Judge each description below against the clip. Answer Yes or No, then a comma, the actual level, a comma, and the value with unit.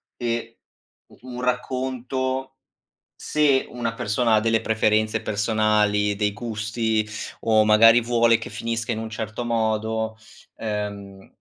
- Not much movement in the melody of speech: Yes, narrow, 1.9 semitones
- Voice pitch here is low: Yes, low, 110 Hz